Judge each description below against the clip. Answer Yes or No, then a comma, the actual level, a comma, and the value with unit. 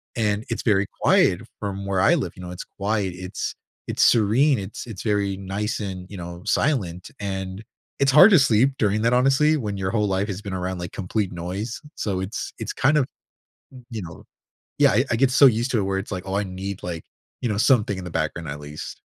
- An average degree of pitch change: Yes, average, 3.7 semitones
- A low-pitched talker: Yes, low, 100 Hz